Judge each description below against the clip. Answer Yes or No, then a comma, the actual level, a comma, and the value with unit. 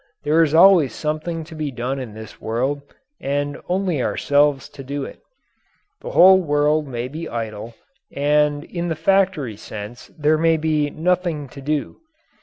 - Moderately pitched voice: Yes, medium, 150 Hz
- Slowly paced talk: No, average, 160 wpm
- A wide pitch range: No, average, 3.3 semitones